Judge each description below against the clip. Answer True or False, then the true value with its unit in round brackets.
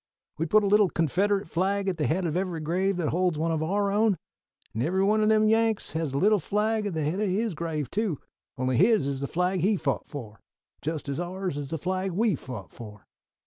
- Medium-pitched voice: True (180 Hz)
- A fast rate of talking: True (230 wpm)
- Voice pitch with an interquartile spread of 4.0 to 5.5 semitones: True (4.7 semitones)